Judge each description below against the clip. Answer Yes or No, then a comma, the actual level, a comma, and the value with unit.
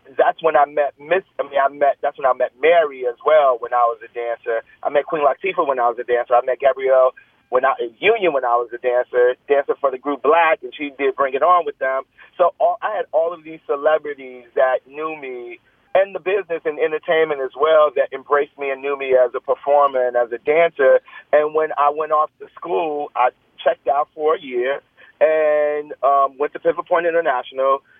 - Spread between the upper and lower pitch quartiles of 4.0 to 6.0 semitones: Yes, average, 4.6 semitones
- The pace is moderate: No, fast, 225 wpm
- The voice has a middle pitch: Yes, medium, 145 Hz